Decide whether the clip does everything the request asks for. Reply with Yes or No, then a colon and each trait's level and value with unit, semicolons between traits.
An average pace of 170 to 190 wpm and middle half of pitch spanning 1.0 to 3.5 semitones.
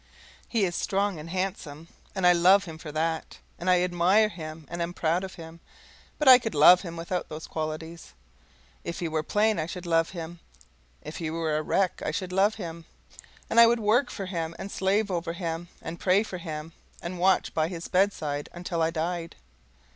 No: average, 200 wpm; average, 2.7 semitones